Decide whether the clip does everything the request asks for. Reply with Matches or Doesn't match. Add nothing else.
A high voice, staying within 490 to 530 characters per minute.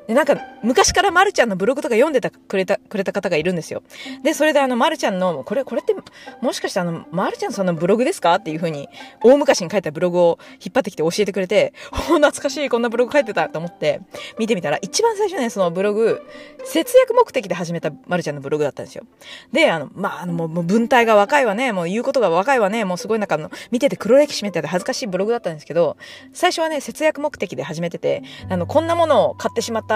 Matches